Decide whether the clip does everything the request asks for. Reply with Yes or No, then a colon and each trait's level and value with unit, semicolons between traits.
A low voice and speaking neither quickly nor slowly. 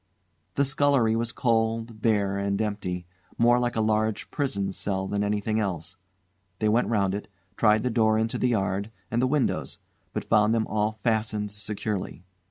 Yes: low, 110 Hz; average, 170 wpm